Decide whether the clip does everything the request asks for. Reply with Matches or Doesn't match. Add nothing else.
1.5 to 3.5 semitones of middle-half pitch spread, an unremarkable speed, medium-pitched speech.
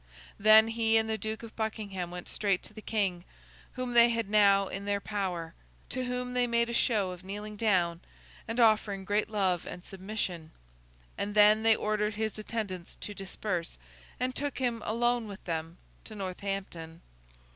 Doesn't match